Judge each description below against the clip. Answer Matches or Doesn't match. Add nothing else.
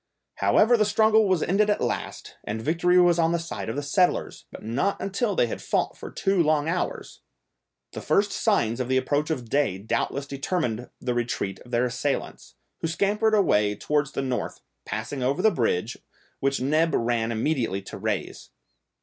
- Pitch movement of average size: Doesn't match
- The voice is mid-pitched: Matches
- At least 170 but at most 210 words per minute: Matches